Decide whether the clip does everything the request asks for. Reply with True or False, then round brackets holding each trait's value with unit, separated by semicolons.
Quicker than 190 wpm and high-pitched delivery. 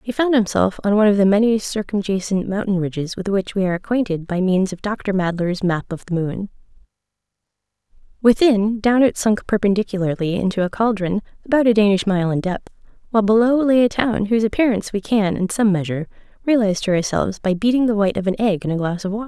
True (205 wpm; 205 Hz)